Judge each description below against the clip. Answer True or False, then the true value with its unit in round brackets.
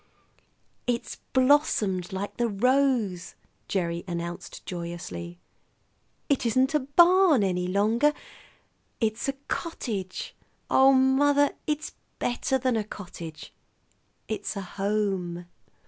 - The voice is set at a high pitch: True (215 Hz)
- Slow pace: True (100 wpm)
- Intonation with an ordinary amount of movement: False (6.7 semitones)